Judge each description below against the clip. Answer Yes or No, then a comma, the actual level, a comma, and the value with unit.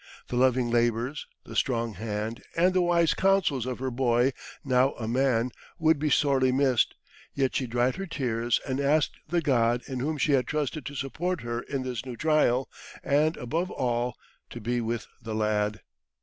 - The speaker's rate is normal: Yes, average, 180 wpm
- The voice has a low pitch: Yes, low, 130 Hz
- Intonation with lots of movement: No, average, 3.7 semitones